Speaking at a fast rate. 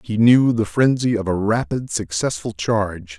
No: average, 170 wpm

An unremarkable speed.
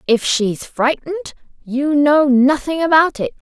No: slow, 120 wpm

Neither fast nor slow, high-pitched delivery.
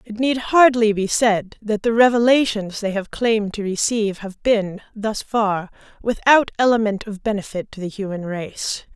Yes: average, 170 wpm; high, 215 Hz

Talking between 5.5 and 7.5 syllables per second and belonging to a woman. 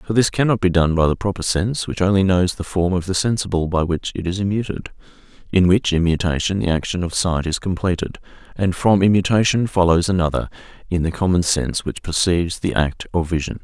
No: 6.0 syllables/s; male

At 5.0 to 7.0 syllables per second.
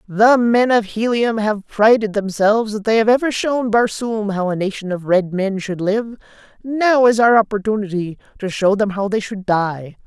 No: 4.7 syllables/s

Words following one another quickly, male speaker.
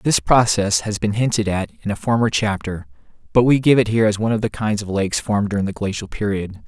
Yes: fast, 245 wpm; male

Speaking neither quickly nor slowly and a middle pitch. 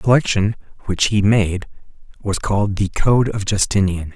No: average, 160 wpm; low, 100 Hz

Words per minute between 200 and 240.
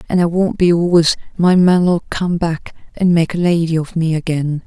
Yes: fast, 205 wpm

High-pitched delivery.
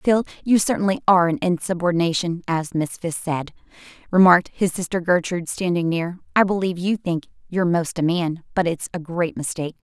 No: medium, 175 Hz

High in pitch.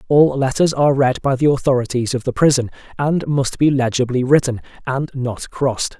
No: low, 135 Hz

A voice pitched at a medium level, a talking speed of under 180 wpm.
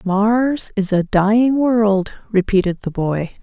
No: high, 205 Hz; average, 140 wpm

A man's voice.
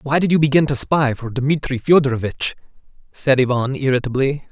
Yes: male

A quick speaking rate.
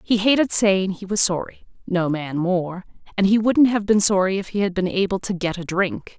Yes: fast, 235 wpm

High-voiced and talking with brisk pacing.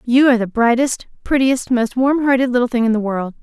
Yes: high, 245 Hz; fast, 230 wpm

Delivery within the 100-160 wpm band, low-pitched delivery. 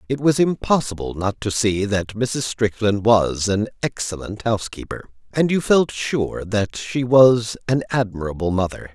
Yes: average, 155 wpm; low, 110 Hz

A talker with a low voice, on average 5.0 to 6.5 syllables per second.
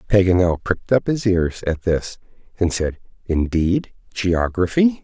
No: very low, 95 Hz; 4.3 syllables/s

